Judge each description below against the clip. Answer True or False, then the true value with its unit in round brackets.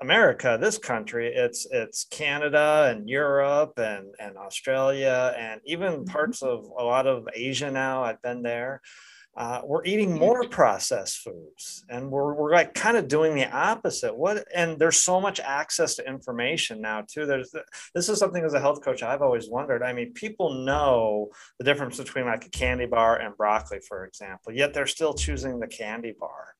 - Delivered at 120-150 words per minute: False (185 wpm)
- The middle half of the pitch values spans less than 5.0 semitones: False (5.6 semitones)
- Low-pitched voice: False (145 Hz)